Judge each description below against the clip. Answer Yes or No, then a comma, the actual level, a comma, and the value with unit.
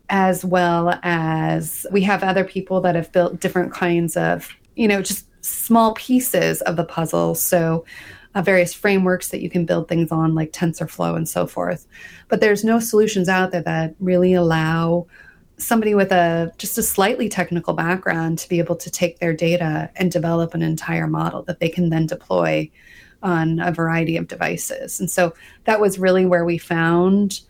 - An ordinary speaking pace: Yes, average, 180 wpm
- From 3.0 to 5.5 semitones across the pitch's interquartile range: No, narrow, 2.4 semitones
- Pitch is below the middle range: No, medium, 175 Hz